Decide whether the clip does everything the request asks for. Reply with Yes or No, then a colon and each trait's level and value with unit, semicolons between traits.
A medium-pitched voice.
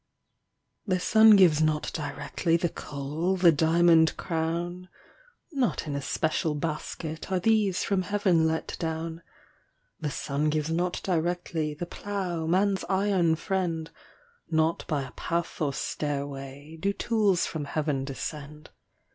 Yes: medium, 165 Hz